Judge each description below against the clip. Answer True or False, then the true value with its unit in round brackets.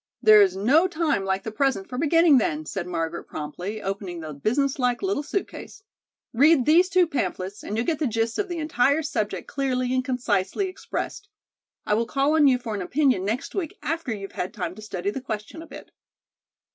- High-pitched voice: True (250 Hz)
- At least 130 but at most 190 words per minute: False (205 wpm)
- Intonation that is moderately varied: False (7.6 semitones)